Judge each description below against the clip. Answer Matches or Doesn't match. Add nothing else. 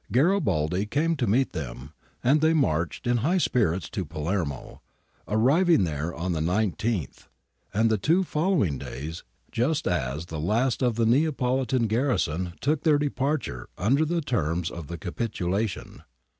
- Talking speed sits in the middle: Matches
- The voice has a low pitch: Matches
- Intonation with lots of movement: Matches